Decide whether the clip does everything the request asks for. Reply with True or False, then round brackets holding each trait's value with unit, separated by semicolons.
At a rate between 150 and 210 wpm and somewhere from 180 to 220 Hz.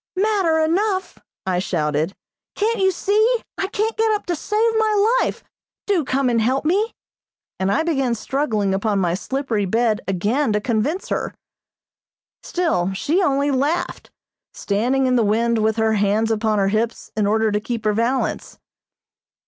False (160 wpm; 245 Hz)